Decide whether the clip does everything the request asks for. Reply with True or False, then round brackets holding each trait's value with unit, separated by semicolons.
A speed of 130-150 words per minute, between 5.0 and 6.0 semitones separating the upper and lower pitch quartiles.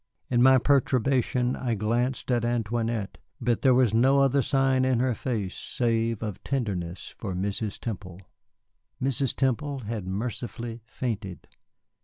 False (135 wpm; 3.2 semitones)